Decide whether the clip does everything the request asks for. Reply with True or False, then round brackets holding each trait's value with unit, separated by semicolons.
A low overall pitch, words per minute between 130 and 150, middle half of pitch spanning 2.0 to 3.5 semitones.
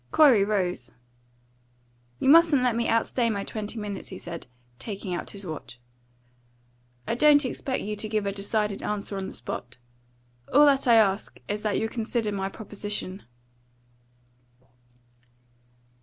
False (210 Hz; 140 wpm; 3.0 semitones)